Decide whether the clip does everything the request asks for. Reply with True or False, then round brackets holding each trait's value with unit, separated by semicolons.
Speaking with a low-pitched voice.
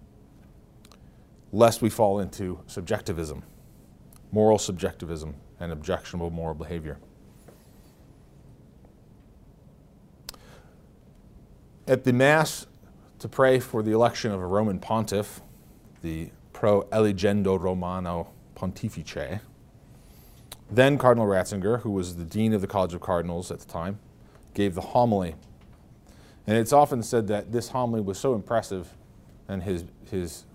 True (100 Hz)